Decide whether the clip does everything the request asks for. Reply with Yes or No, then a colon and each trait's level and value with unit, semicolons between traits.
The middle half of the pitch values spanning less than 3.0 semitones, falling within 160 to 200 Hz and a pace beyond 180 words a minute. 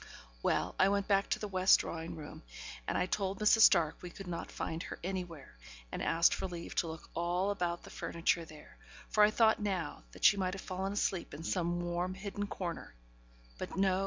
Yes: narrow, 2.6 semitones; medium, 185 Hz; fast, 205 wpm